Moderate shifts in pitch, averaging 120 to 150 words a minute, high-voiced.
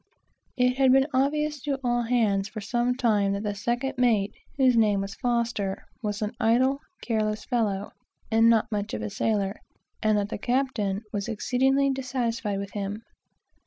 No: average, 3.5 semitones; average, 165 wpm; high, 230 Hz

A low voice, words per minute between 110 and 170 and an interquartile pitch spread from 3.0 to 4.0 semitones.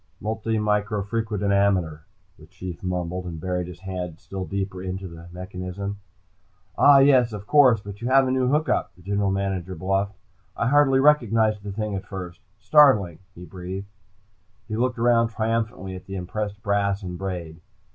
Yes: low, 100 Hz; average, 155 wpm; average, 3.4 semitones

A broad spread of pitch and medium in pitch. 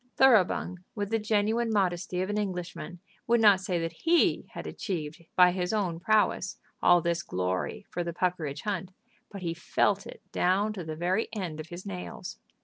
No: average, 3.4 semitones; medium, 180 Hz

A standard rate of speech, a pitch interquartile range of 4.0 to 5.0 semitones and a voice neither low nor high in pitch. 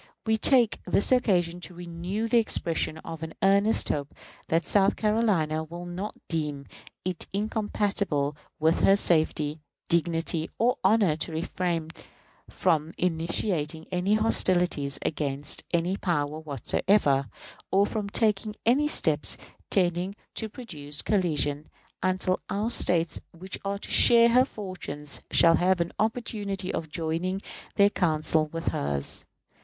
No: slow, 130 wpm; average, 4.3 semitones; medium, 175 Hz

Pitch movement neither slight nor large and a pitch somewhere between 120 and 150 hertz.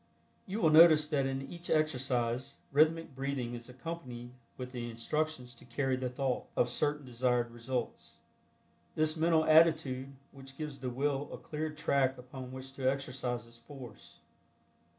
Yes: average, 3.6 semitones; low, 135 Hz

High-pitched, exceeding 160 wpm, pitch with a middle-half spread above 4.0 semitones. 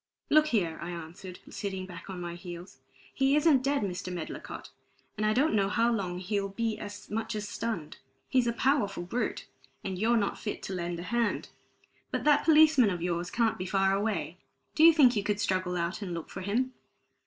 Yes: high, 200 Hz; average, 200 wpm; average, 4.7 semitones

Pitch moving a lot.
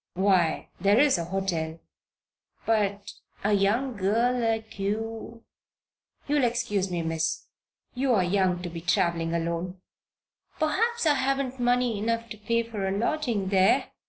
No: average, 4.7 semitones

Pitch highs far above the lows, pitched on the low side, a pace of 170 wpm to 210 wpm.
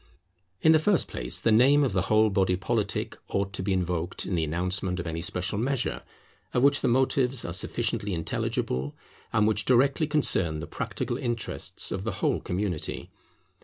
Yes: wide, 5.9 semitones; low, 105 Hz; average, 175 wpm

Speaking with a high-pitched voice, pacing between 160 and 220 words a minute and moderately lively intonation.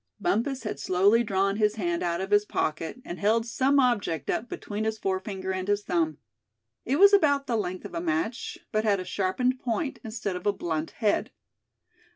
Yes: high, 205 Hz; average, 195 wpm; average, 4.1 semitones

